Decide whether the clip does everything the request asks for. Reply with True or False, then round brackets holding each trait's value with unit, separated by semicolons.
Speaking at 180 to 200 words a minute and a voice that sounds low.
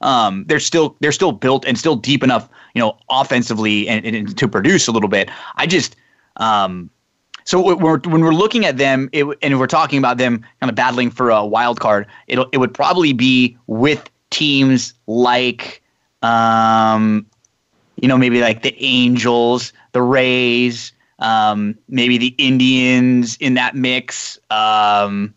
False (165 wpm; 125 Hz)